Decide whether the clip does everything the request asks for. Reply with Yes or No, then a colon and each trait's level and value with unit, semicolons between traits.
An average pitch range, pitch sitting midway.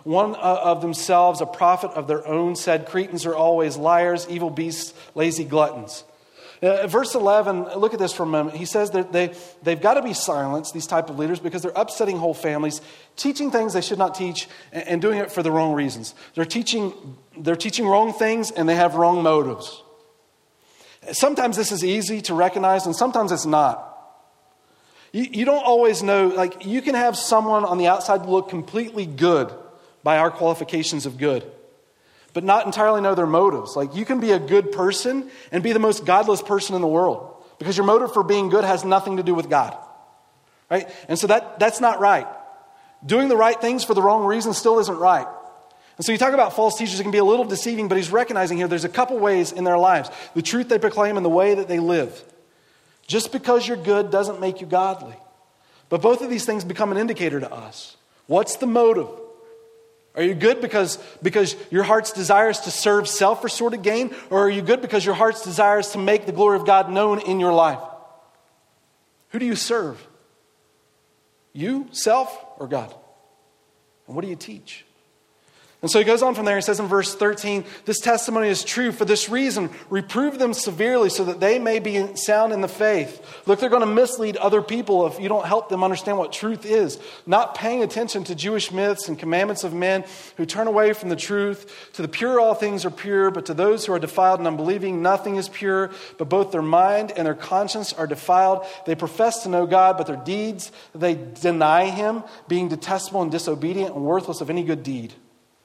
No: average, 3.9 semitones; high, 195 Hz